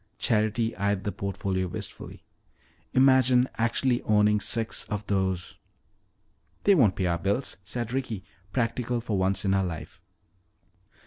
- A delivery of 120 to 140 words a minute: Yes, slow, 135 wpm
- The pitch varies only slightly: No, average, 3.9 semitones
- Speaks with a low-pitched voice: Yes, low, 105 Hz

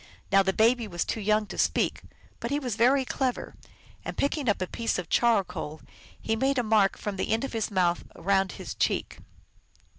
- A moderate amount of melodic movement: Yes, average, 4.0 semitones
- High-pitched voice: Yes, high, 220 Hz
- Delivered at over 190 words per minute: Yes, average, 200 wpm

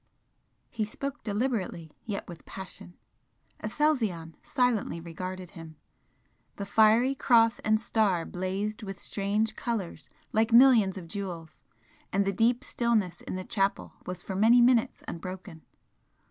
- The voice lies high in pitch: Yes, high, 205 Hz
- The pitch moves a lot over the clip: No, average, 3.8 semitones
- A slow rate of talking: Yes, slow, 130 wpm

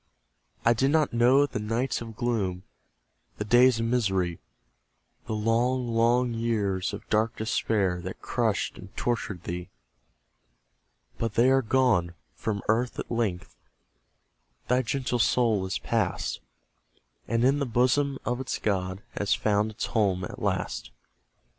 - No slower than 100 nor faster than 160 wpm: Yes, average, 140 wpm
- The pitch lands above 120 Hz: No, low, 115 Hz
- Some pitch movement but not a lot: Yes, average, 3.4 semitones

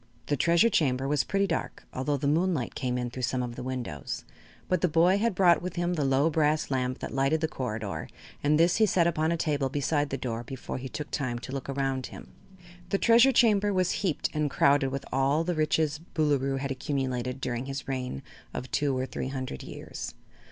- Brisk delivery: Yes, fast, 215 wpm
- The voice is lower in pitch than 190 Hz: Yes, medium, 140 Hz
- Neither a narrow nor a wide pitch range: Yes, average, 4.1 semitones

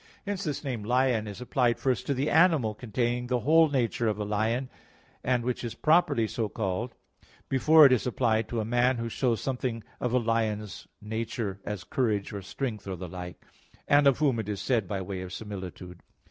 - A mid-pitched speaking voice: No, low, 115 Hz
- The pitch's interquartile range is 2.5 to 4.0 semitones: Yes, average, 3.5 semitones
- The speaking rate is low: No, average, 200 wpm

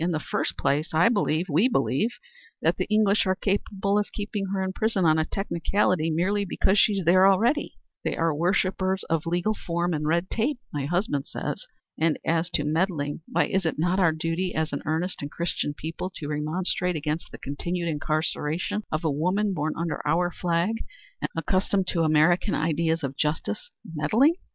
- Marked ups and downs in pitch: No, average, 3.6 semitones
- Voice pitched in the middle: Yes, medium, 170 Hz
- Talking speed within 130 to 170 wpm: No, average, 185 wpm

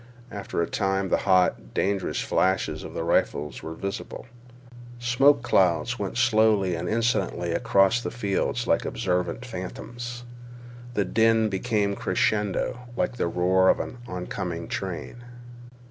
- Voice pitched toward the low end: Yes, low, 100 Hz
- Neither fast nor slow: No, slow, 130 wpm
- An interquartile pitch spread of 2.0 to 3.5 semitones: No, average, 4.0 semitones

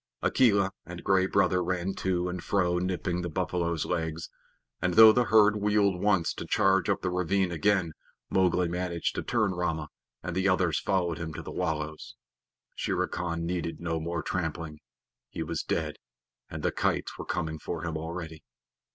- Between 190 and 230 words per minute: No, average, 170 wpm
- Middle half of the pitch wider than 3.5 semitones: No, narrow, 2.4 semitones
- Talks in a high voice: No, very low, 90 Hz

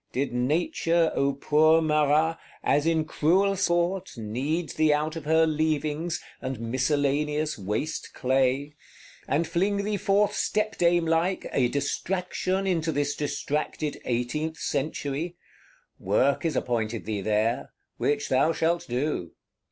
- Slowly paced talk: Yes, slow, 120 wpm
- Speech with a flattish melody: No, average, 3.5 semitones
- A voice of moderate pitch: Yes, medium, 150 Hz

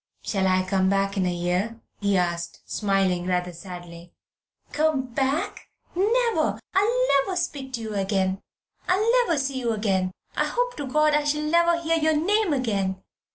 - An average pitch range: No, wide, 8.9 semitones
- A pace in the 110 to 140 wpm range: No, average, 165 wpm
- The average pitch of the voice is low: No, high, 230 Hz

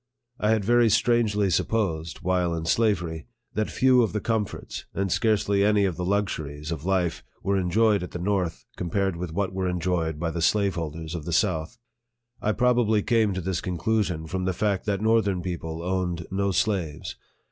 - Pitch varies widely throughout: No, average, 3.7 semitones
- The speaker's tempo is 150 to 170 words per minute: No, average, 180 wpm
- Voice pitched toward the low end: Yes, very low, 95 Hz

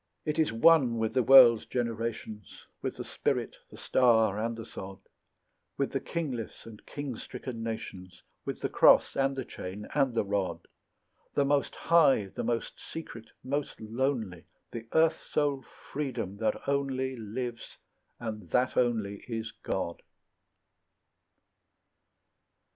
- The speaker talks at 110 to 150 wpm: Yes, slow, 135 wpm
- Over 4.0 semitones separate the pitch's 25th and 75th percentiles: No, average, 3.7 semitones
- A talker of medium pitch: No, low, 115 Hz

